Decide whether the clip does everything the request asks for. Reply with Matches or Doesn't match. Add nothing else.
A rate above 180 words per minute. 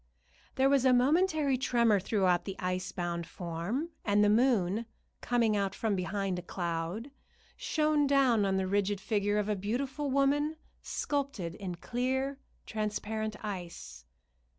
Doesn't match